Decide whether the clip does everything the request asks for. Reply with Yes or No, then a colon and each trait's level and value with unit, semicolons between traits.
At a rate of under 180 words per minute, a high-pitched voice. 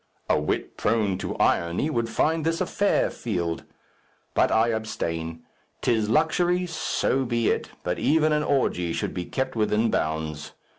No: average, 155 wpm; low, 115 Hz